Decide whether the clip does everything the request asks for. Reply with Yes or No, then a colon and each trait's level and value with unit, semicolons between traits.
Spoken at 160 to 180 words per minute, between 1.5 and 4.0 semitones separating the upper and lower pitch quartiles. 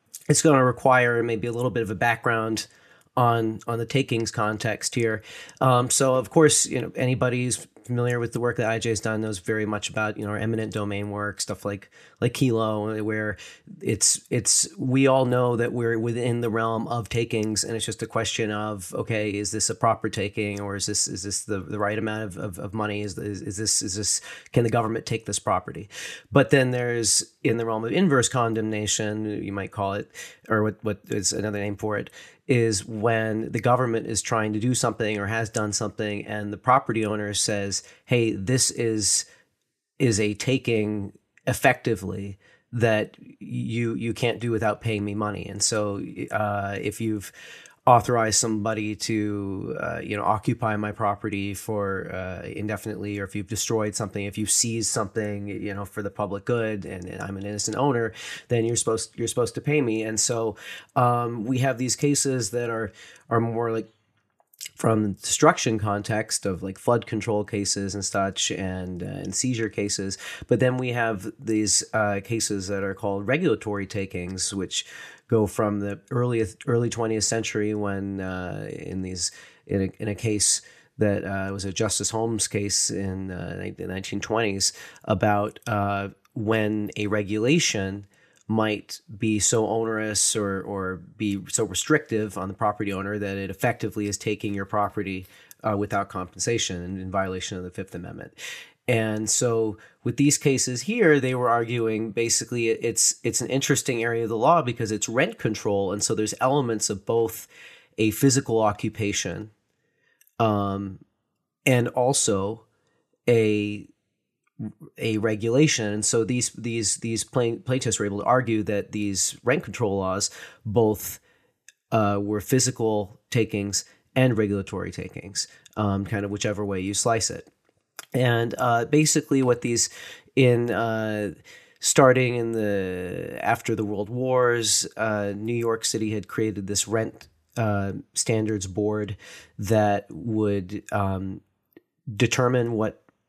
Yes: average, 170 wpm; narrow, 2.4 semitones